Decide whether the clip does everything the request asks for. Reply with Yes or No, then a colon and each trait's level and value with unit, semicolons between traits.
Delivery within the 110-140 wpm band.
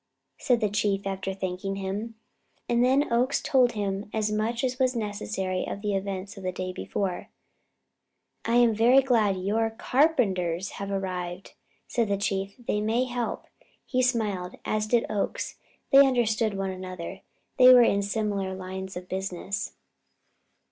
No: average, 155 wpm